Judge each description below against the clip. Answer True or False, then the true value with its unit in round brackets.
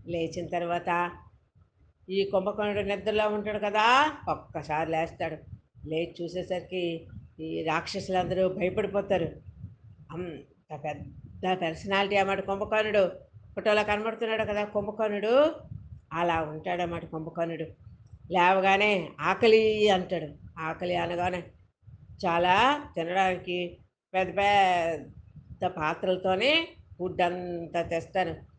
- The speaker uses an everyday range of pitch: True (3.5 semitones)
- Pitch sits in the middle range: True (180 Hz)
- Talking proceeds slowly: False (85 wpm)